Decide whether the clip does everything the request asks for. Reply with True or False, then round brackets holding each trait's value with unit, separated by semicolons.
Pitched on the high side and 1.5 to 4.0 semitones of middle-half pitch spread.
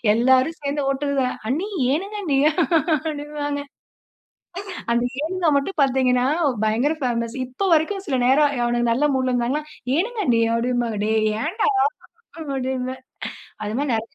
True (270 Hz; 3.6 semitones)